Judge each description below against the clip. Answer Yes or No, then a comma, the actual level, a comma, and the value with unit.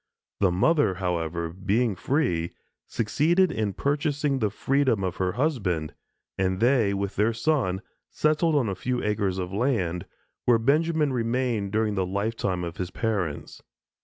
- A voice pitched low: Yes, low, 110 Hz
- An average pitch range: No, wide, 6.5 semitones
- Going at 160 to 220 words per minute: No, average, 145 wpm